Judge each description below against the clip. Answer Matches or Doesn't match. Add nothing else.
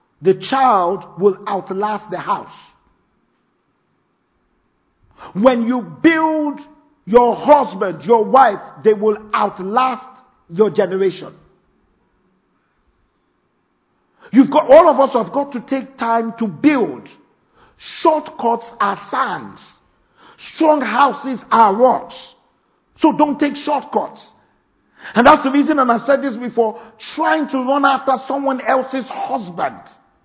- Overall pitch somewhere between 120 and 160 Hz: Doesn't match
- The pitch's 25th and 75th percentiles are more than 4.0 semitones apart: Matches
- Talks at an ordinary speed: Doesn't match